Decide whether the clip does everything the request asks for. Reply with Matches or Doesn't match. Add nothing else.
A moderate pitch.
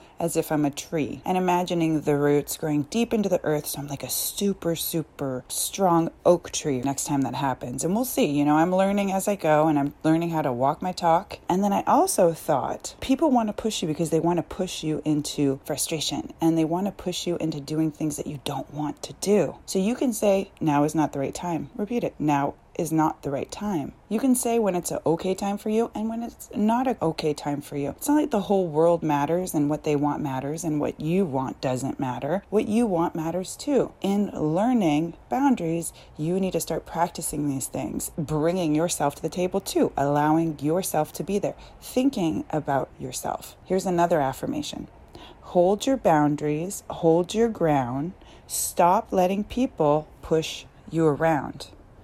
Matches